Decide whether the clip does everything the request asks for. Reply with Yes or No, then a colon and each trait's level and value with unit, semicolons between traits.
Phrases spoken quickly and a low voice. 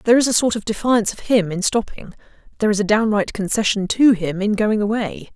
No: fast, 225 wpm; high, 210 Hz